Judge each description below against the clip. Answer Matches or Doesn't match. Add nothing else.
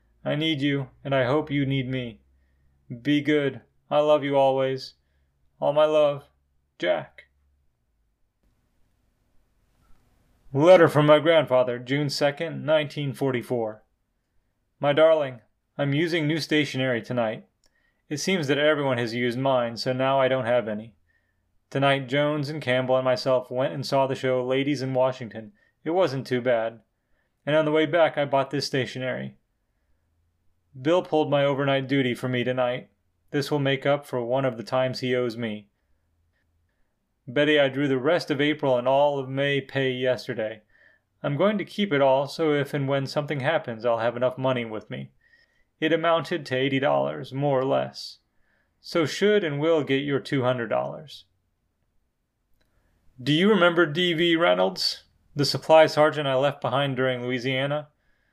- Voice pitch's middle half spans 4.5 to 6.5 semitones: Doesn't match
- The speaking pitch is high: Doesn't match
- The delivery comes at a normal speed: Matches